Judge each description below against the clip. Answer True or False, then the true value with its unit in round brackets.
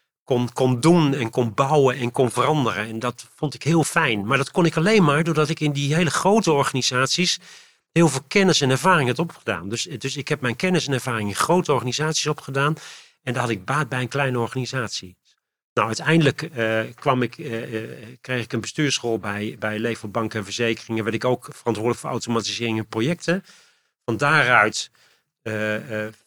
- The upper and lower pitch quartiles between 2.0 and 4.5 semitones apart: False (5.1 semitones)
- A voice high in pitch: False (130 Hz)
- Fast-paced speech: False (190 wpm)